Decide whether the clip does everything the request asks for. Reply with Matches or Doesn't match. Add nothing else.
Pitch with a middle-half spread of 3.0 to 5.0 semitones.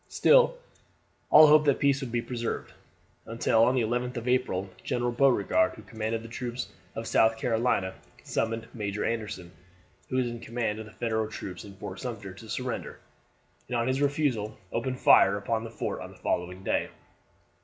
Doesn't match